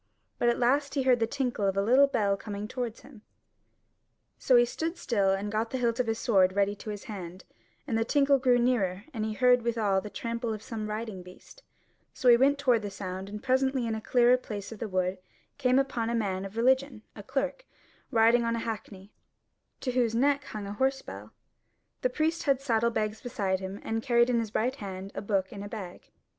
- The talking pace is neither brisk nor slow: No, fast, 220 wpm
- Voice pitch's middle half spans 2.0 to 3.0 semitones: No, average, 3.7 semitones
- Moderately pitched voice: No, high, 230 Hz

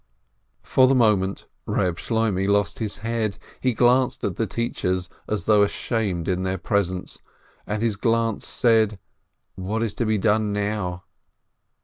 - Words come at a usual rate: Yes, average, 145 wpm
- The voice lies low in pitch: Yes, low, 105 Hz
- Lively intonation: No, average, 3.1 semitones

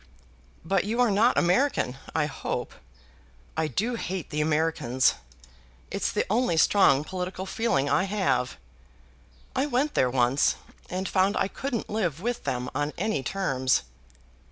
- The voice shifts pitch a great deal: Yes, wide, 6.9 semitones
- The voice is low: No, medium, 185 Hz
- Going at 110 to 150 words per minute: Yes, average, 140 wpm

